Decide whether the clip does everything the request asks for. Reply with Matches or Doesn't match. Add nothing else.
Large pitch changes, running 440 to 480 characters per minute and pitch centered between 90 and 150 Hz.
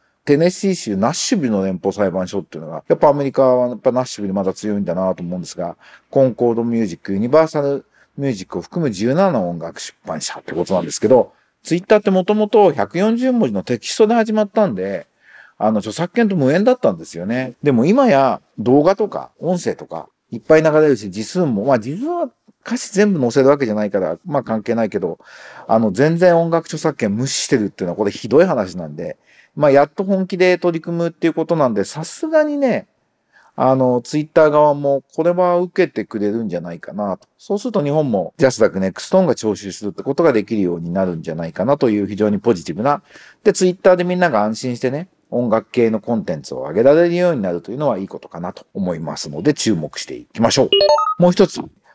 Matches